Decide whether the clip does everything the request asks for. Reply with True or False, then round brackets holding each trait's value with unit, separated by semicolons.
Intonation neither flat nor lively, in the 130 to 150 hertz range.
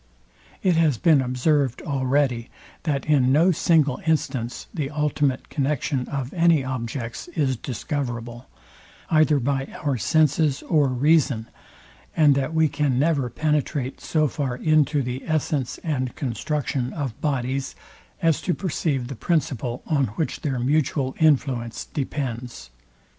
True (3.3 semitones; 140 Hz)